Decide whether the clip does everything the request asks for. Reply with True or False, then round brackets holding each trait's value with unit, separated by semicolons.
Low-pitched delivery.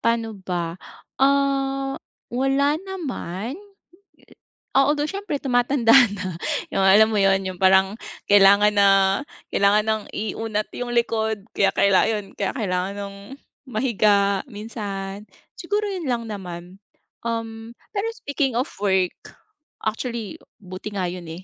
False (215 Hz)